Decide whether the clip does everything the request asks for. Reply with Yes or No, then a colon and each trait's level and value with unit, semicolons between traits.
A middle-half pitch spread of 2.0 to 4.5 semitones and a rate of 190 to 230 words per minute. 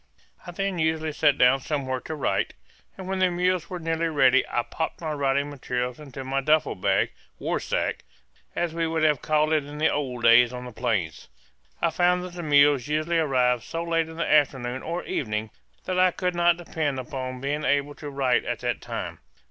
Yes: average, 4.1 semitones; average, 200 wpm